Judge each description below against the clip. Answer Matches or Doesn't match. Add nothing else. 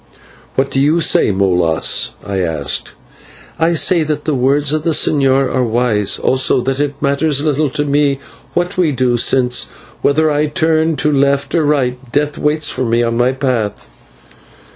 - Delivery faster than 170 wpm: Doesn't match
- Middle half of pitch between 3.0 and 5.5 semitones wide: Matches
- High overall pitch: Doesn't match